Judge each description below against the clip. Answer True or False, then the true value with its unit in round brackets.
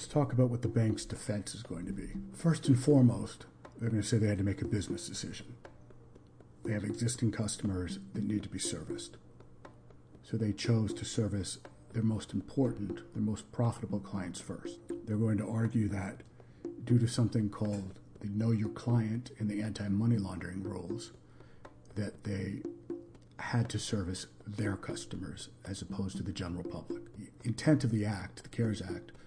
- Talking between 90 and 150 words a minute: False (175 wpm)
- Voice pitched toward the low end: True (105 Hz)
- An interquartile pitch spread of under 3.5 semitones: True (2.9 semitones)